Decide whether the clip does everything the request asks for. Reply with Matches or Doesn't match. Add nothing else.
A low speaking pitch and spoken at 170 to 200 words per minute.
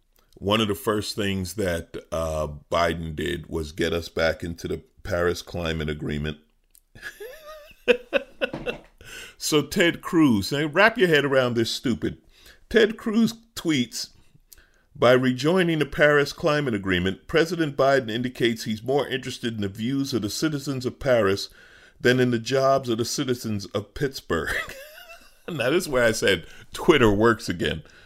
Doesn't match